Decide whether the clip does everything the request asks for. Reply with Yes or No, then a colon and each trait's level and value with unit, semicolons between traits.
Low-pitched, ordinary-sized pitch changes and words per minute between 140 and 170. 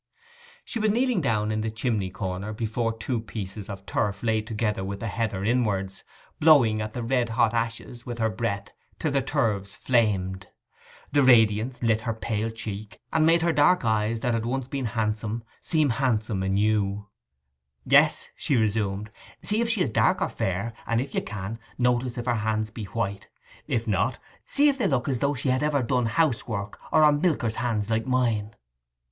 No: low, 115 Hz; average, 3.2 semitones; average, 185 wpm